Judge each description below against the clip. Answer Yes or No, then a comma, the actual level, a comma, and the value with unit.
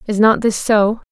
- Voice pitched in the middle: No, high, 215 Hz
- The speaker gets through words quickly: Yes, fast, 215 wpm